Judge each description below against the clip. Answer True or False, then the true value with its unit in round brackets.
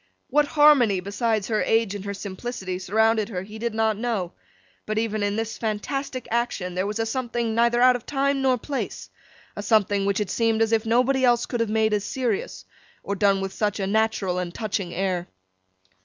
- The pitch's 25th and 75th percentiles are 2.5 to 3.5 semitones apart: True (3.0 semitones)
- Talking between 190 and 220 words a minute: True (200 wpm)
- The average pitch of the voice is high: True (220 Hz)